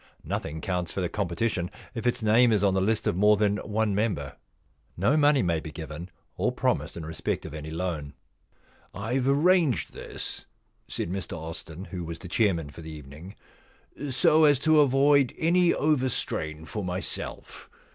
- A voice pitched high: No, low, 100 Hz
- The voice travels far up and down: Yes, wide, 7.4 semitones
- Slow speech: No, average, 175 wpm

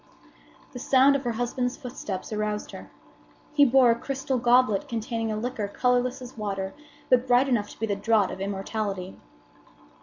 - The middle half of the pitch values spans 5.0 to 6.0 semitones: No, average, 3.3 semitones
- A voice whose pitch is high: Yes, high, 235 Hz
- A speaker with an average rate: Yes, average, 170 wpm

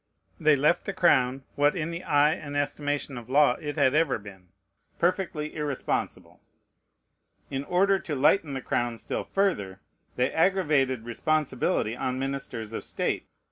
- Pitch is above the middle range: No, medium, 145 Hz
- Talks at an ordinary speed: Yes, average, 145 wpm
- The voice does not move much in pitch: No, average, 3.4 semitones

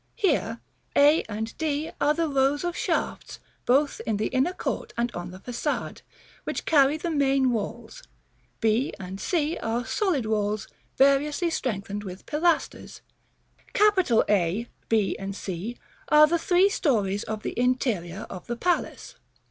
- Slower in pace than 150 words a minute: Yes, average, 140 wpm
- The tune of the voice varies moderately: No, wide, 6.1 semitones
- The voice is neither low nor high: No, very high, 255 Hz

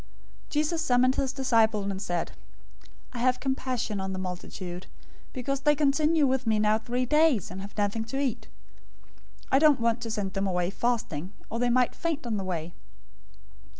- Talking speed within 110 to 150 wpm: No, average, 180 wpm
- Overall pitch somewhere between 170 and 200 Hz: No, high, 235 Hz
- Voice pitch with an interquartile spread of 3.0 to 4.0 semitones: No, average, 5.2 semitones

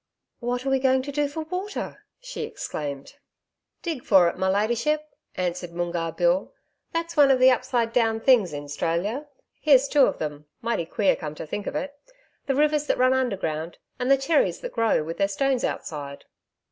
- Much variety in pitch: Yes, wide, 8.1 semitones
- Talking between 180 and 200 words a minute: Yes, average, 185 wpm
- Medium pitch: No, high, 235 Hz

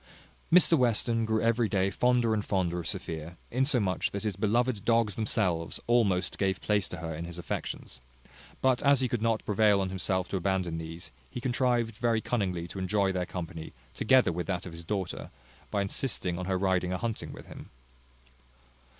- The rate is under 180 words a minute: No, average, 185 wpm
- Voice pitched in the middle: No, low, 100 Hz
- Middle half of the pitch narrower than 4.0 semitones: No, average, 4.4 semitones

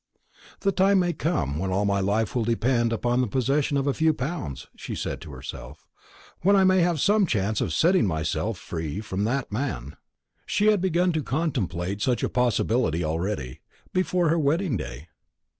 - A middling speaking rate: Yes, average, 180 wpm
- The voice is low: Yes, low, 125 Hz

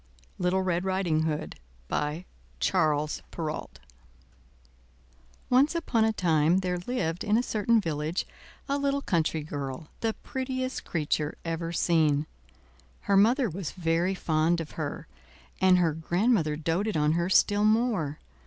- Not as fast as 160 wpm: Yes, slow, 135 wpm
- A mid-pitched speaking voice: Yes, medium, 175 Hz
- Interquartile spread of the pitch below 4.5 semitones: No, average, 5.3 semitones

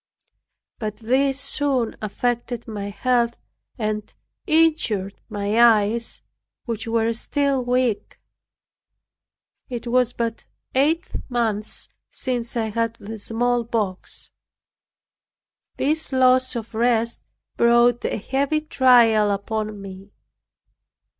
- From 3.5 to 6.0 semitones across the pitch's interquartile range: No, average, 2.7 semitones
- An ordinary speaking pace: No, slow, 95 wpm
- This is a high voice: Yes, high, 235 Hz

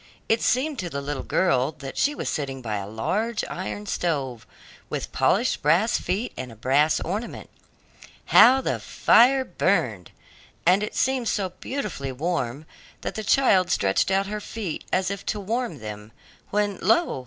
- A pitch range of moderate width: No, wide, 8.2 semitones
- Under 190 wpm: Yes, average, 160 wpm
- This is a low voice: No, medium, 185 Hz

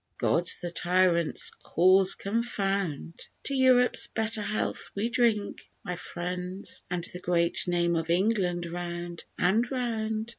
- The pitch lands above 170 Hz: Yes, medium, 185 Hz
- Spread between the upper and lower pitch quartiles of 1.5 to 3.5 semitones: No, average, 4.0 semitones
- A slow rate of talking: Yes, slow, 125 wpm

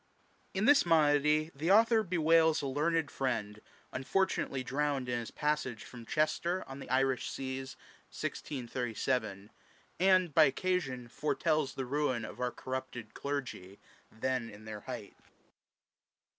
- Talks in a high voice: No, low, 135 Hz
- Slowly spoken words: Yes, slow, 130 wpm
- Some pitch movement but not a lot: Yes, average, 4.3 semitones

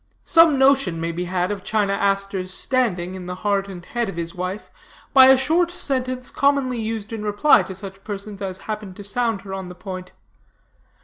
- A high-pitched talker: Yes, high, 200 Hz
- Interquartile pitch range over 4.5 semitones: Yes, average, 5.2 semitones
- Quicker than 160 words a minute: Yes, average, 195 wpm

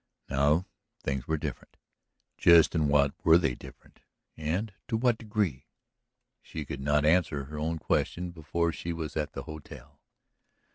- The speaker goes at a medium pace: Yes, average, 150 wpm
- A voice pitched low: Yes, very low, 80 Hz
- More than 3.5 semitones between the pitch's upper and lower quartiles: No, average, 2.8 semitones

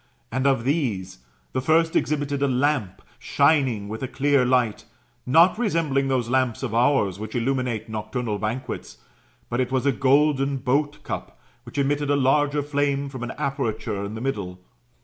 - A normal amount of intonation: Yes, average, 3.6 semitones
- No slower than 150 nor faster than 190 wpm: Yes, average, 165 wpm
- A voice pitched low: Yes, low, 130 Hz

